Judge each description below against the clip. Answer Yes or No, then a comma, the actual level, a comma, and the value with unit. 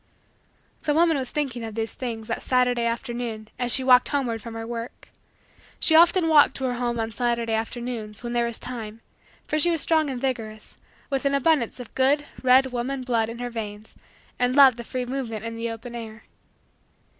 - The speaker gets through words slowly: No, average, 195 wpm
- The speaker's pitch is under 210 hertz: No, high, 245 Hz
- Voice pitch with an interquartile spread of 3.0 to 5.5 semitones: No, narrow, 2.6 semitones